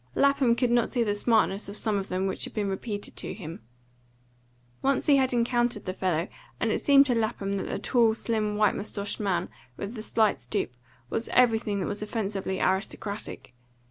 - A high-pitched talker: Yes, high, 215 Hz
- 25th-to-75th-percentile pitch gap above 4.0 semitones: No, average, 3.2 semitones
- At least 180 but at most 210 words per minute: Yes, average, 190 wpm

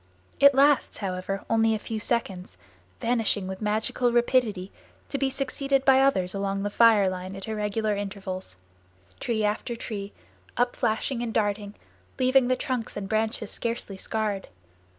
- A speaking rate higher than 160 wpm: No, average, 145 wpm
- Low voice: No, high, 220 Hz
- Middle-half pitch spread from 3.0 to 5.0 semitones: Yes, average, 3.5 semitones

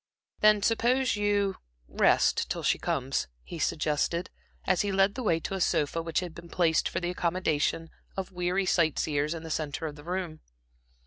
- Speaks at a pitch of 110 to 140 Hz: No, medium, 175 Hz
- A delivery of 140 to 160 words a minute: No, average, 190 wpm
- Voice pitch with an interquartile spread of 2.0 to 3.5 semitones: Yes, average, 3.2 semitones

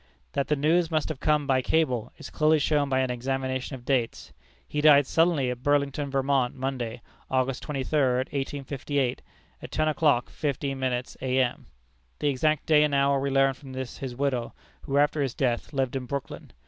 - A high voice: No, low, 135 Hz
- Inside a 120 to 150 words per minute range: No, average, 180 wpm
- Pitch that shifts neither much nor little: No, narrow, 2.1 semitones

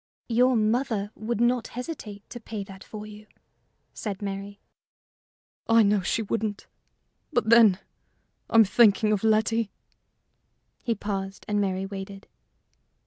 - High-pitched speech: Yes, high, 215 Hz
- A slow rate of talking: Yes, slow, 125 wpm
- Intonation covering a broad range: No, narrow, 2.4 semitones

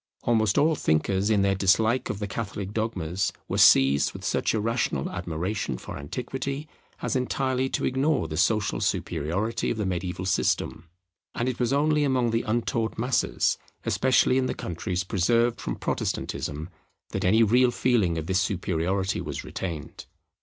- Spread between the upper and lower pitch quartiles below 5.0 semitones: No, average, 5.3 semitones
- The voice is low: Yes, low, 105 Hz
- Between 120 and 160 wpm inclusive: Yes, average, 155 wpm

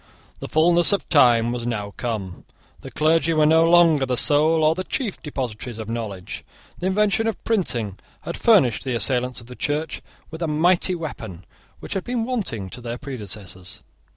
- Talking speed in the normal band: Yes, average, 180 wpm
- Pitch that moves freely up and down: Yes, wide, 6.7 semitones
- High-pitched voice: No, medium, 145 Hz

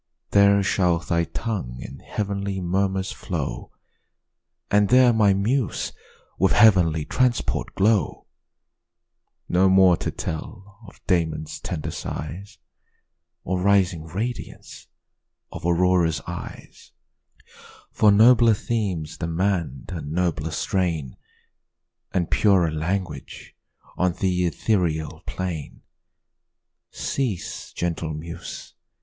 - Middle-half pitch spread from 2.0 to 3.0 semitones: No, average, 3.5 semitones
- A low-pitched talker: Yes, very low, 90 Hz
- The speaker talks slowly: Yes, slow, 95 wpm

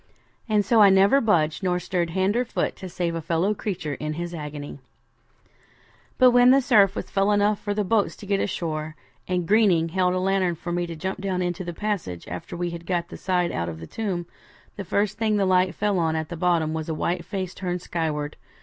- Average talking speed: No, fast, 220 wpm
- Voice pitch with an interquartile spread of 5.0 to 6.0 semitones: No, average, 3.3 semitones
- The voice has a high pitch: No, medium, 180 Hz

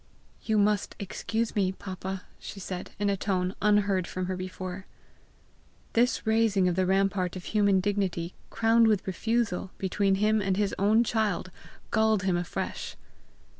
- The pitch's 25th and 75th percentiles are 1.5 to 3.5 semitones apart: Yes, narrow, 2.4 semitones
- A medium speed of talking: Yes, average, 150 wpm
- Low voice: No, high, 195 Hz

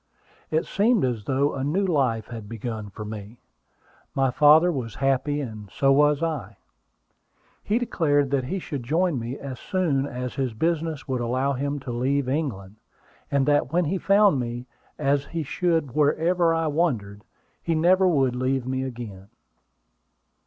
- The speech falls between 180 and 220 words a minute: No, average, 160 wpm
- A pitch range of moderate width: Yes, average, 4.8 semitones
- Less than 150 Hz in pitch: Yes, medium, 140 Hz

